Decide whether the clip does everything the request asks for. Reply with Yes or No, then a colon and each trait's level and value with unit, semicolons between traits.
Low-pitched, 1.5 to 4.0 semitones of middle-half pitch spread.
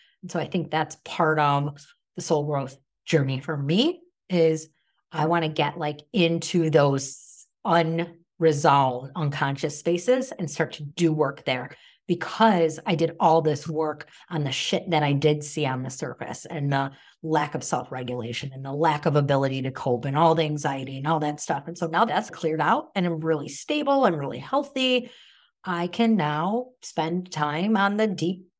No: medium, 160 Hz; average, 3.1 semitones